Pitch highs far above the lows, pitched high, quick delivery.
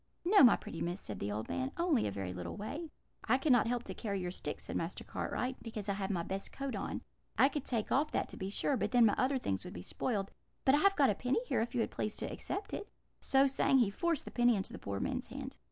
Yes: wide, 5.9 semitones; high, 240 Hz; fast, 265 wpm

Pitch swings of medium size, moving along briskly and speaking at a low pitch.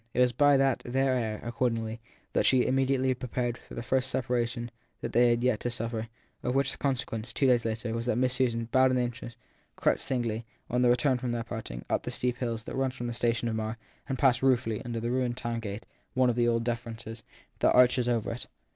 No: narrow, 1.7 semitones; fast, 225 wpm; low, 120 Hz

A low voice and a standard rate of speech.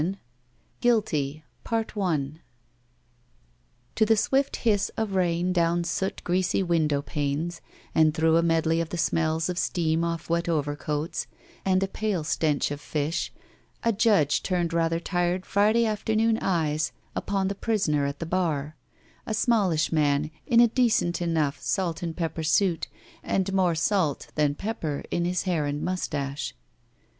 No: medium, 170 Hz; average, 150 wpm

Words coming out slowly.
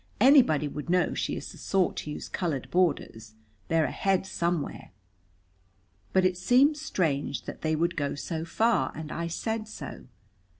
No: average, 160 wpm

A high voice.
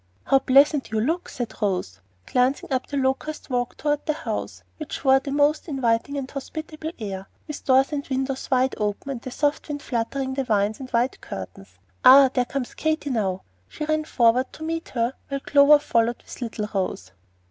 Yes: very high, 265 Hz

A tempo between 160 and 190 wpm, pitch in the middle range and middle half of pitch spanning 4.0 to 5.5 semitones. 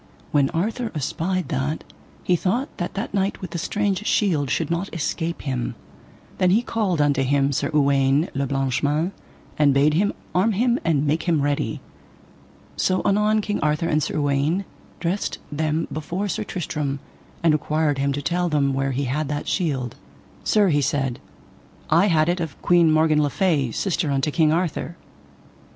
Yes: average, 170 wpm; medium, 155 Hz; average, 4.3 semitones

